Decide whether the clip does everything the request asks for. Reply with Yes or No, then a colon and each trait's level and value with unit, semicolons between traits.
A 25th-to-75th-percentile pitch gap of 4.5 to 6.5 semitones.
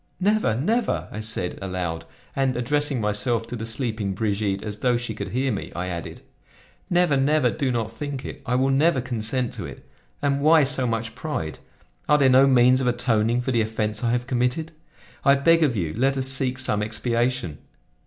No: average, 3.8 semitones